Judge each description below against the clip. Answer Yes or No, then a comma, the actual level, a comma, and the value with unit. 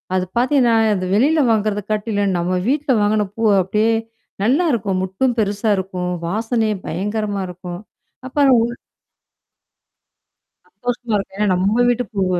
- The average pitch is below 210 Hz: No, high, 215 Hz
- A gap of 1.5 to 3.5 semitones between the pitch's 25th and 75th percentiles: No, average, 3.9 semitones